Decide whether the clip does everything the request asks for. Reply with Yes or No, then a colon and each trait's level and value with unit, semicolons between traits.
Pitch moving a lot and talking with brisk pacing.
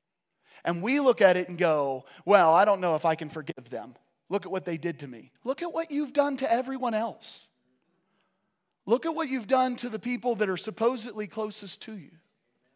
Yes: wide, 5.9 semitones; fast, 210 wpm